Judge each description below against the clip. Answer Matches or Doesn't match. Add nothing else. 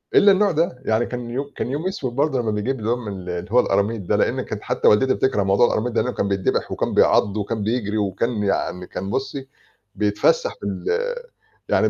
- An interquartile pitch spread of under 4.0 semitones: Doesn't match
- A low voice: Matches